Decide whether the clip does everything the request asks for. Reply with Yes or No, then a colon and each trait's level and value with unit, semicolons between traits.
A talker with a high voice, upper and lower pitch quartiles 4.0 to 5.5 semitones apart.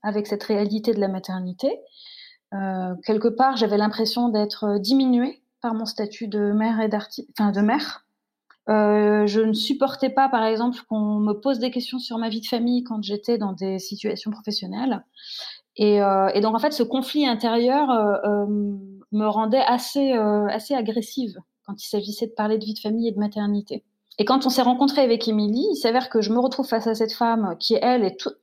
No: high, 220 Hz; average, 3.2 semitones